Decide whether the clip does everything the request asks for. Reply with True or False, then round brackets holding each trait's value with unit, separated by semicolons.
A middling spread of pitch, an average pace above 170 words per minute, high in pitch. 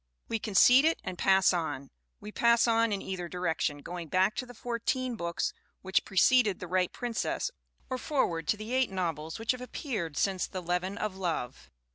True (4.9 semitones; 200 wpm; 195 Hz)